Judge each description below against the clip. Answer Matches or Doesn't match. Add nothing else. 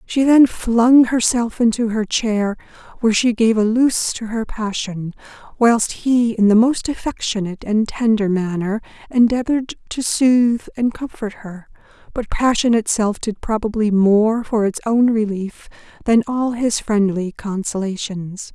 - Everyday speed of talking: Matches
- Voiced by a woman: Matches